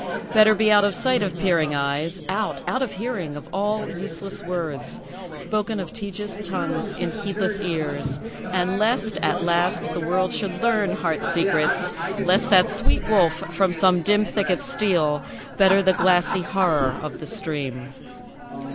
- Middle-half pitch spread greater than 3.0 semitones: Yes, average, 3.6 semitones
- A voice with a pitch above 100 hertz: Yes, medium, 185 Hz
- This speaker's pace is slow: No, average, 155 wpm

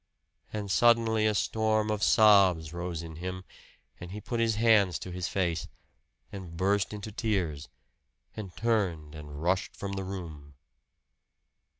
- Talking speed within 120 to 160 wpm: Yes, average, 140 wpm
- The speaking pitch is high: No, very low, 95 Hz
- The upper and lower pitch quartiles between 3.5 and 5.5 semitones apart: Yes, average, 3.9 semitones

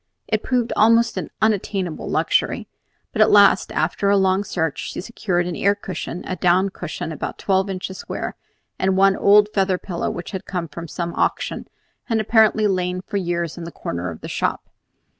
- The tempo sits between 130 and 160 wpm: No, average, 190 wpm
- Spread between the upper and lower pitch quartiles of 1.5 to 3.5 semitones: Yes, narrow, 2.6 semitones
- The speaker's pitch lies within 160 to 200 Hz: Yes, high, 190 Hz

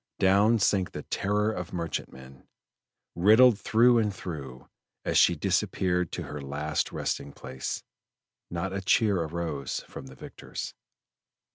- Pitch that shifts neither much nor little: No, wide, 6.1 semitones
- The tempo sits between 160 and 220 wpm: No, slow, 135 wpm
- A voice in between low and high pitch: No, very low, 90 Hz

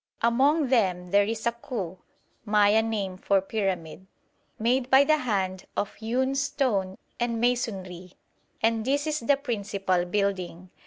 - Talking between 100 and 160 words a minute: Yes, average, 140 wpm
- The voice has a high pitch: Yes, high, 220 Hz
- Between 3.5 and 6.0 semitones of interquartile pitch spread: Yes, average, 4.7 semitones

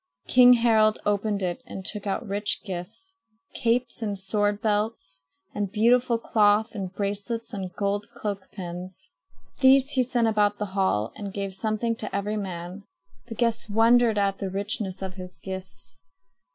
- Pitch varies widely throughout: No, average, 2.8 semitones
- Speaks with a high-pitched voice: Yes, high, 205 Hz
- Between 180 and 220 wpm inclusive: No, average, 155 wpm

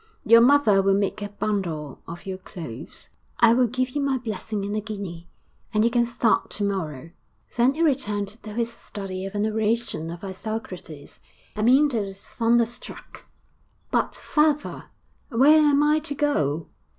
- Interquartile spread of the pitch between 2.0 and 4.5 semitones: Yes, average, 4.2 semitones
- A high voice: Yes, high, 215 Hz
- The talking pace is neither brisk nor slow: Yes, average, 160 wpm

